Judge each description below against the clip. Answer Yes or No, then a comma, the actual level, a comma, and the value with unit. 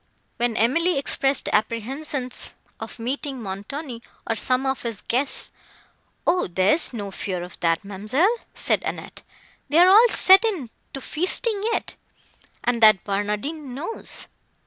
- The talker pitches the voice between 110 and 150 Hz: No, very high, 255 Hz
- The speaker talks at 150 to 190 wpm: No, average, 140 wpm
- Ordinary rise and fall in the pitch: No, wide, 6.6 semitones